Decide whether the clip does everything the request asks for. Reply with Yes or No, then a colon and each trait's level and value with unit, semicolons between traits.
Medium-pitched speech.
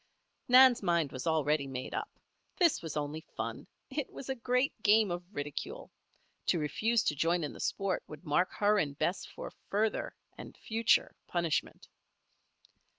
Yes: medium, 180 Hz